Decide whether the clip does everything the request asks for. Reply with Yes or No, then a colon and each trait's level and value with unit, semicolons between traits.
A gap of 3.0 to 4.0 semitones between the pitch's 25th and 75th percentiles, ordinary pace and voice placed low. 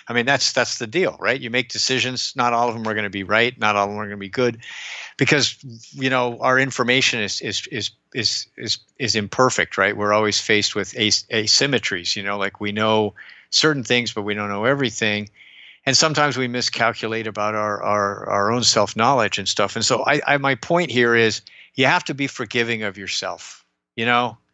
No: average, 3.5 semitones; fast, 215 wpm; low, 115 Hz